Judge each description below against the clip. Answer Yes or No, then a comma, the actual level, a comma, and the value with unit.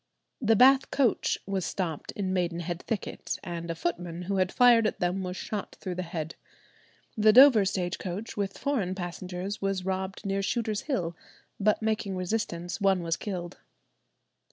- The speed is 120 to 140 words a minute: No, average, 160 wpm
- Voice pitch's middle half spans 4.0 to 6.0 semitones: No, average, 3.3 semitones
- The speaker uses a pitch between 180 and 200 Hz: Yes, high, 190 Hz